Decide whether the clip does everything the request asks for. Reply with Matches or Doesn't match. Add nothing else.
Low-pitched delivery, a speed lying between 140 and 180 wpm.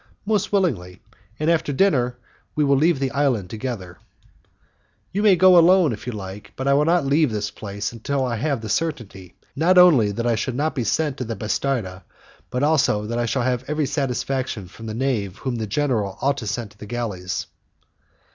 Doesn't match